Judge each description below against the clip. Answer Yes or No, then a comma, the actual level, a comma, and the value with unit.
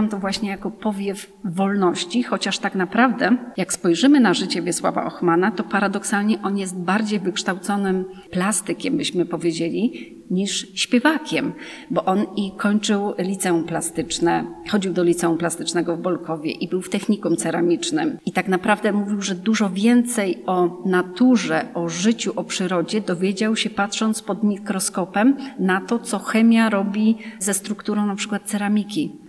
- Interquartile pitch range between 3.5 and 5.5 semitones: No, average, 2.8 semitones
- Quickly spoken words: No, average, 145 wpm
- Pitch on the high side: Yes, high, 200 Hz